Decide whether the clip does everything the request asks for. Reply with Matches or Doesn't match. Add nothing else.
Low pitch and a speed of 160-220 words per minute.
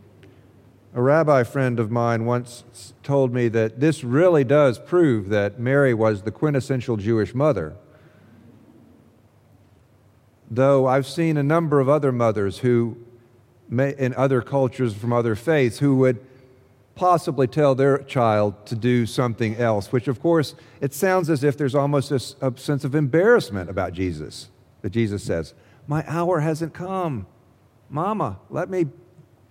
Doesn't match